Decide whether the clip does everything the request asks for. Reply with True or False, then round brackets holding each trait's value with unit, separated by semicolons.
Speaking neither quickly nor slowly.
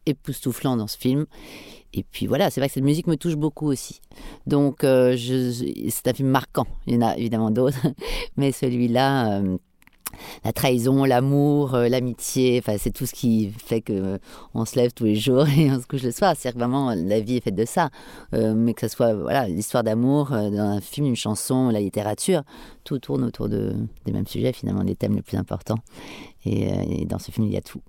False (225 wpm)